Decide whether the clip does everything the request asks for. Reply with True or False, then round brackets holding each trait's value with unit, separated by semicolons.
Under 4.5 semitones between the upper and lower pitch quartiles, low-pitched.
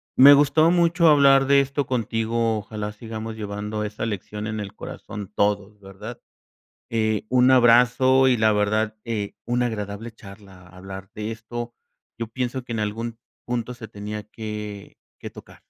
True (2.8 semitones; 110 Hz)